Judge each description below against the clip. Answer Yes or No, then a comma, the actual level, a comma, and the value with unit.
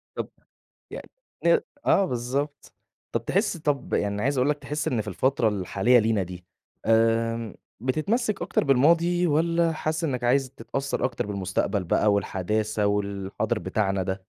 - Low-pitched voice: Yes, low, 120 Hz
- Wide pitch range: Yes, wide, 6.4 semitones